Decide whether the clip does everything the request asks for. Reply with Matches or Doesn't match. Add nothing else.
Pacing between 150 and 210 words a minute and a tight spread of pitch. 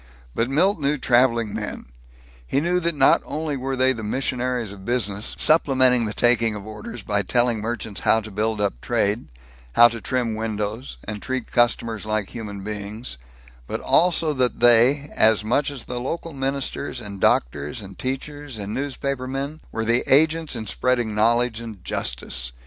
Doesn't match